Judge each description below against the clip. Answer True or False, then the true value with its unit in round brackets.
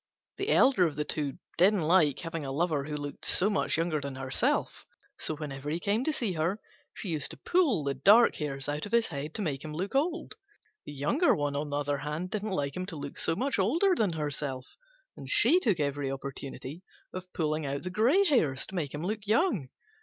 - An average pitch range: False (6.3 semitones)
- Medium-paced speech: False (215 wpm)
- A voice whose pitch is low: False (160 Hz)